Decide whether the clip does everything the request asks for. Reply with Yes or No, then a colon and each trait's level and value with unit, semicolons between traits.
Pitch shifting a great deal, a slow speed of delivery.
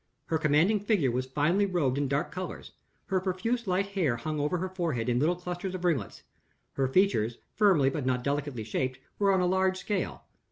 No: wide, 5.8 semitones; average, 195 wpm